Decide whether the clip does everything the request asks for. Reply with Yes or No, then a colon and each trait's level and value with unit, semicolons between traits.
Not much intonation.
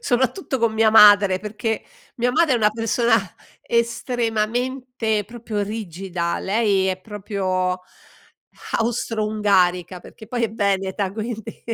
No: average, 3.1 semitones